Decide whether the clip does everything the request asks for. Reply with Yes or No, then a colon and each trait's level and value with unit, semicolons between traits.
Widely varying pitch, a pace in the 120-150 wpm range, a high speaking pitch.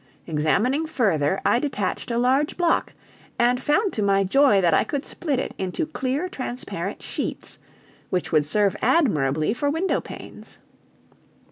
Yes: wide, 7.3 semitones; average, 145 wpm; high, 245 Hz